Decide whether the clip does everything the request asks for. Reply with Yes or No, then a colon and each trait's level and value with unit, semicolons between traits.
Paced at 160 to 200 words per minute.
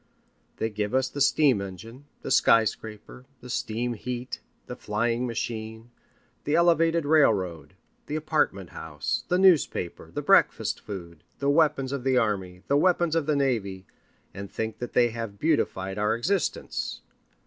No: average, 150 wpm